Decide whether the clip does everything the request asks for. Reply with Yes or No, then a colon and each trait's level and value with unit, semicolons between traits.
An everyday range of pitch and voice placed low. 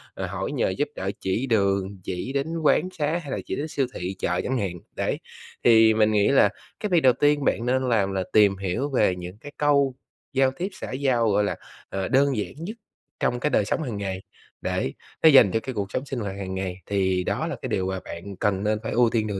No: wide, 5.7 semitones; low, 110 Hz